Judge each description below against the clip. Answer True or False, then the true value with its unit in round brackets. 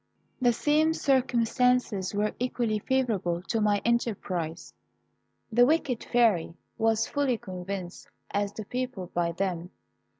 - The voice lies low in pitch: False (220 Hz)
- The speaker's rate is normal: False (125 wpm)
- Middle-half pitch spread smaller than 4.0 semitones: False (4.9 semitones)